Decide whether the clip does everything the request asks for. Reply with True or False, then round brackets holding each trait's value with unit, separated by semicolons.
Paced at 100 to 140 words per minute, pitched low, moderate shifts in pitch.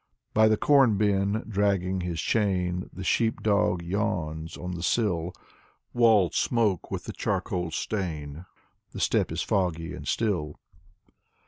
True (135 wpm; 95 Hz; 3.7 semitones)